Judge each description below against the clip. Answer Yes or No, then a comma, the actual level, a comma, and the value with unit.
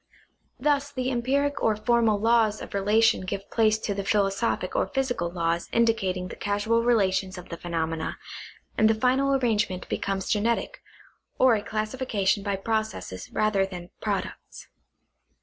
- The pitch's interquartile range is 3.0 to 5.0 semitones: Yes, average, 3.5 semitones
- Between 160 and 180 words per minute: No, average, 140 wpm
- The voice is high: Yes, high, 215 Hz